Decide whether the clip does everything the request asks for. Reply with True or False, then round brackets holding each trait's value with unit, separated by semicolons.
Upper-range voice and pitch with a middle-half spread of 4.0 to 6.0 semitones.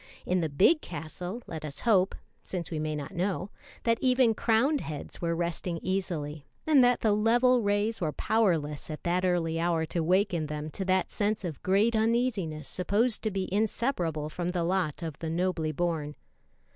False (180 Hz; 5.2 semitones)